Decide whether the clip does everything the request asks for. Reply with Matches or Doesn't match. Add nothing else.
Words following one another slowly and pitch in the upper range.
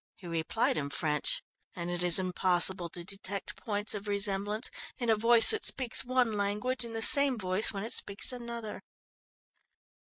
Doesn't match